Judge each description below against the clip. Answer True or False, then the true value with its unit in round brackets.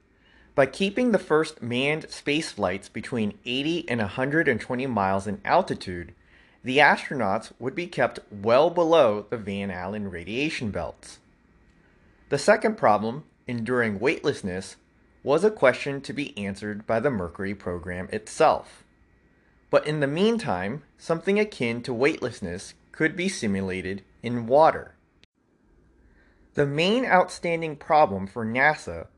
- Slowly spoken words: True (125 wpm)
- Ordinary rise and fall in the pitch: False (7.6 semitones)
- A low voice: True (125 Hz)